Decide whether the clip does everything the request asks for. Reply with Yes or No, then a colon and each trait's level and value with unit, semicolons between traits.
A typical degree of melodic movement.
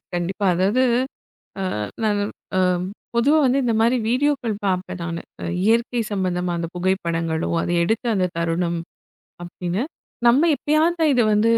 No: wide, 5.7 semitones